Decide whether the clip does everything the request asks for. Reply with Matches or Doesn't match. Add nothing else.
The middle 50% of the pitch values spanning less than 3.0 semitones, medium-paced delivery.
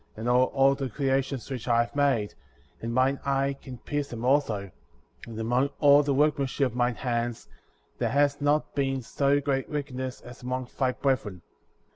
Matches